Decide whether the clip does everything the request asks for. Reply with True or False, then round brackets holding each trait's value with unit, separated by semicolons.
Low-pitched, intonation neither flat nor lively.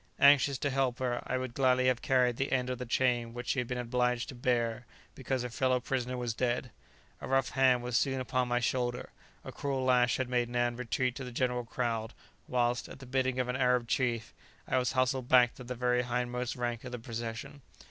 False (125 Hz; 1.0 semitones)